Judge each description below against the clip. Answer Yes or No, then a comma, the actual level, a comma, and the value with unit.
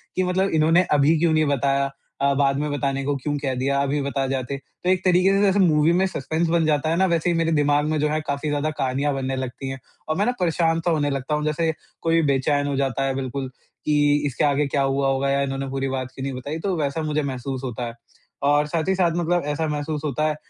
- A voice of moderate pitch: Yes, medium, 145 Hz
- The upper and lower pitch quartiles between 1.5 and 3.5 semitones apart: Yes, average, 2.9 semitones